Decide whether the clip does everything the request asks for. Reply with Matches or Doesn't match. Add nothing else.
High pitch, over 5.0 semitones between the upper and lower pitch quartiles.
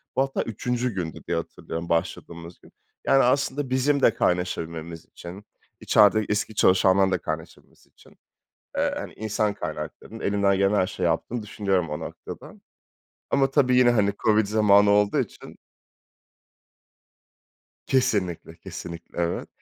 Doesn't match